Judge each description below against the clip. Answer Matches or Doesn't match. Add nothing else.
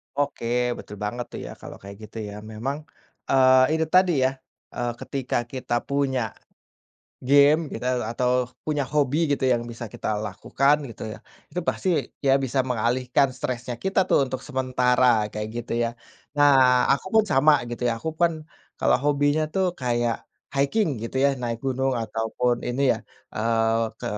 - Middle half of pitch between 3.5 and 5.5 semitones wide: Doesn't match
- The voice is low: Matches